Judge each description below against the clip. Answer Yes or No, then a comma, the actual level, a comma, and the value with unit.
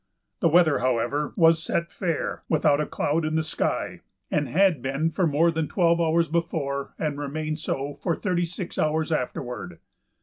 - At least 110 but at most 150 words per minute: No, average, 170 wpm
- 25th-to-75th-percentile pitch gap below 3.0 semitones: Yes, narrow, 2.6 semitones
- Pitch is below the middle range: No, medium, 160 Hz